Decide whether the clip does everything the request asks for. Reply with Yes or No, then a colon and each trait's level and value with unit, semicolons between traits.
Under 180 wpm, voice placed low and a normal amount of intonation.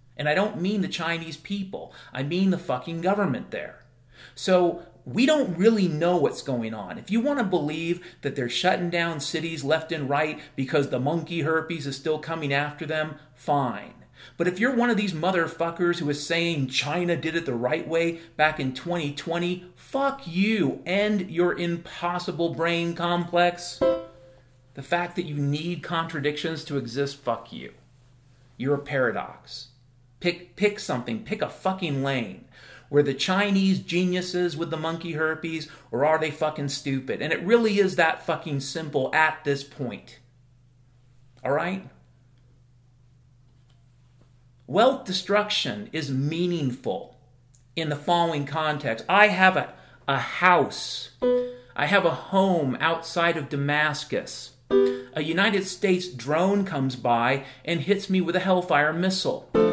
No: average, 150 wpm; medium, 160 Hz; average, 4.9 semitones